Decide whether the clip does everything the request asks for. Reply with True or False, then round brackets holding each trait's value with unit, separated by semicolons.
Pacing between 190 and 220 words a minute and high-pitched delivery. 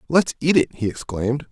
False (200 wpm; 135 Hz)